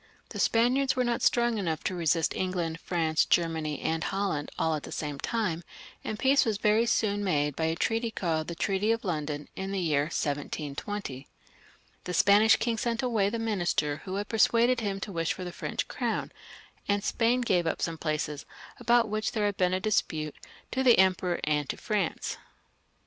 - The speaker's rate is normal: Yes, average, 185 wpm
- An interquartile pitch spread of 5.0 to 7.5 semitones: Yes, wide, 5.6 semitones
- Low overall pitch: No, high, 190 Hz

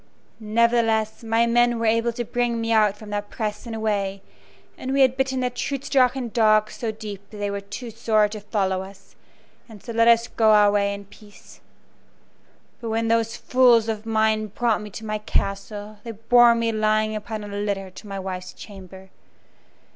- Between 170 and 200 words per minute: Yes, average, 190 wpm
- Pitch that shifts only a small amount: Yes, narrow, 2.1 semitones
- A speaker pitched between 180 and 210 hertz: No, high, 220 Hz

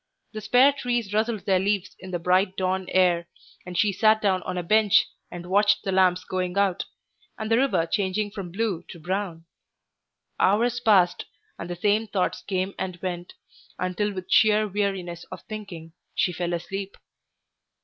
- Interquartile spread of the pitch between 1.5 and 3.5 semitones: Yes, average, 2.8 semitones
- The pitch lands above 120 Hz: Yes, high, 190 Hz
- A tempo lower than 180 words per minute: Yes, average, 170 wpm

